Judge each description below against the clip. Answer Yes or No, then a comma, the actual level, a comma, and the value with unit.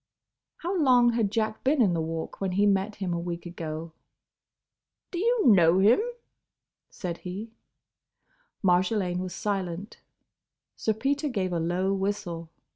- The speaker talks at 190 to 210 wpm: No, average, 140 wpm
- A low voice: No, high, 195 Hz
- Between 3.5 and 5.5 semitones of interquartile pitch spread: Yes, average, 4.1 semitones